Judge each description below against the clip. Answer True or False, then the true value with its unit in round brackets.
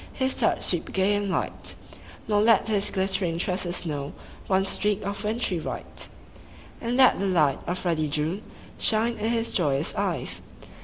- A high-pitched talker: True (195 Hz)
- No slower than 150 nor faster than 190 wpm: True (160 wpm)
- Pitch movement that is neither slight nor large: True (3.9 semitones)